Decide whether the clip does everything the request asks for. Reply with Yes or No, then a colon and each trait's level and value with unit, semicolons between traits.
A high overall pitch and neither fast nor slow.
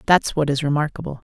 No: medium, 150 Hz; average, 185 wpm